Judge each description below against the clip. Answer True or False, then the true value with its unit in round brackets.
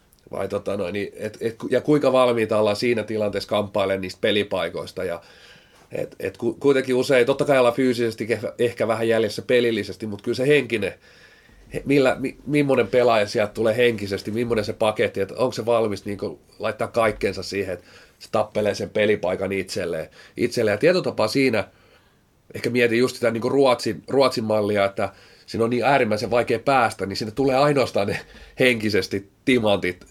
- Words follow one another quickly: True (165 wpm)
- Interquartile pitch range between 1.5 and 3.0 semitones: False (3.4 semitones)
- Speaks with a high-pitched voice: False (115 Hz)